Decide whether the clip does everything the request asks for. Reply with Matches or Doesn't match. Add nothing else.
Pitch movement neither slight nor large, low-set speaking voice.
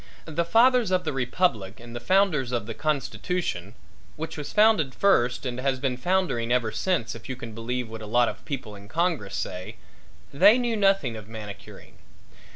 Doesn't match